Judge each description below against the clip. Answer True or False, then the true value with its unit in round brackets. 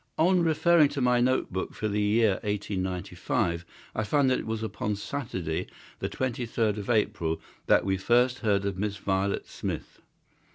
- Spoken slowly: False (165 wpm)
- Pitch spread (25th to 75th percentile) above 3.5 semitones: True (4.2 semitones)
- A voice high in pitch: False (105 Hz)